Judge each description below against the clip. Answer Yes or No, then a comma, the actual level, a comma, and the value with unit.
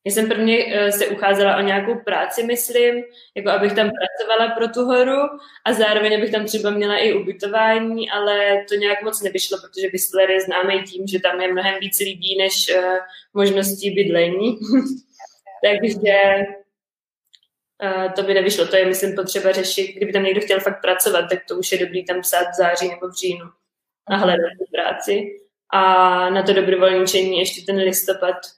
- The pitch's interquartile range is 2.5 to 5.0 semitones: No, narrow, 2.1 semitones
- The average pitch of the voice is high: Yes, high, 195 Hz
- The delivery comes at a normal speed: No, fast, 175 wpm